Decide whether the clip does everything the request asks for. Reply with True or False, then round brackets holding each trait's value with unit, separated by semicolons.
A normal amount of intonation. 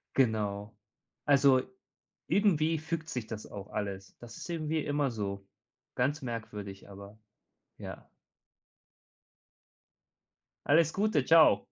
False (7.2 semitones)